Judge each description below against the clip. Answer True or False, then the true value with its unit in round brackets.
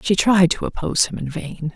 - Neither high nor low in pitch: True (165 Hz)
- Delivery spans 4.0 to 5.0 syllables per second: False (5.5 syllables/s)